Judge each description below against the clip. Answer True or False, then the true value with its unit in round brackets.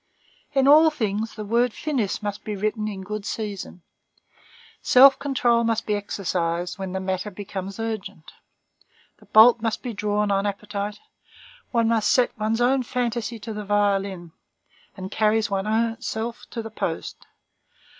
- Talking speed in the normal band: True (150 wpm)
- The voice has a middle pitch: False (215 Hz)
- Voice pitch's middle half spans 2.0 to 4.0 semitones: True (2.6 semitones)